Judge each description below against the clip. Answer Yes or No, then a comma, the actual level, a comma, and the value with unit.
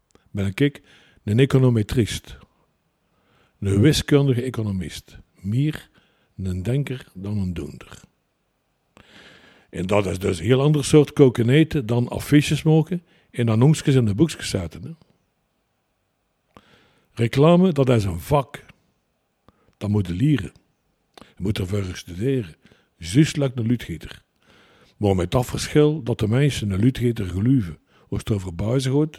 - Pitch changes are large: Yes, wide, 6.3 semitones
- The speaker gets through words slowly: Yes, slow, 130 wpm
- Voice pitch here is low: Yes, low, 120 Hz